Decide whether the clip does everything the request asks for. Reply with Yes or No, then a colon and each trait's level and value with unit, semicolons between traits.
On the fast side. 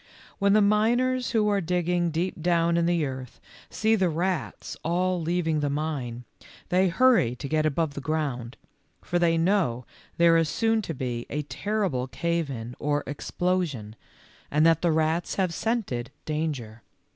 No: average, 165 wpm